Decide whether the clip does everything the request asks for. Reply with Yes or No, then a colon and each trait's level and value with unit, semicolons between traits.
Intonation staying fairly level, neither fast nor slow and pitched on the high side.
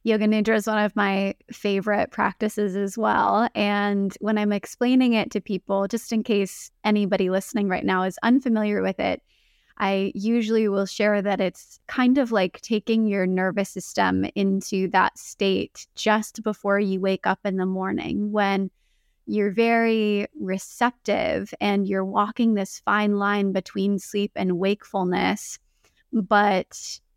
Yes: narrow, 1.8 semitones; average, 150 wpm; high, 205 Hz